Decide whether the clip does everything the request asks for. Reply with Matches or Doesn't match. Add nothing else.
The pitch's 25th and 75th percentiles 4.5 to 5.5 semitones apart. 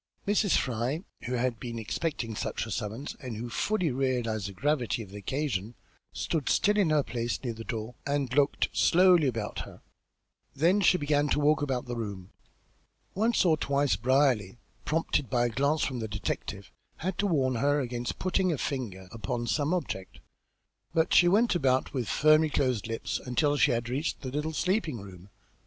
Matches